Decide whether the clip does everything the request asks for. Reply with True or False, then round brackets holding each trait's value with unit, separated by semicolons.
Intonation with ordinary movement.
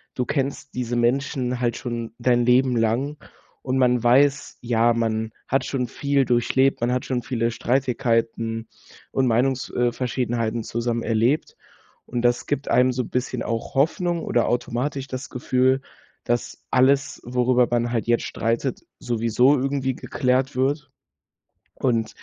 False (2.0 semitones)